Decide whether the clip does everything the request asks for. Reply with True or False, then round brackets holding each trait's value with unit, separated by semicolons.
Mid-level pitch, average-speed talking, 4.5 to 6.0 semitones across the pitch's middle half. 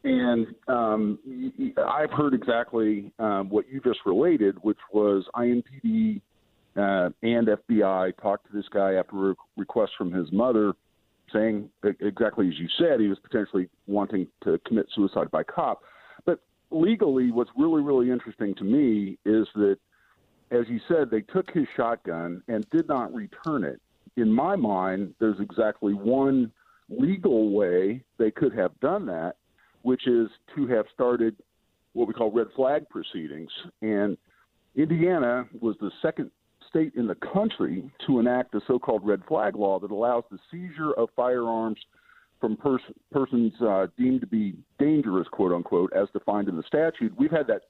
False (115 Hz; 160 wpm; 5.1 semitones)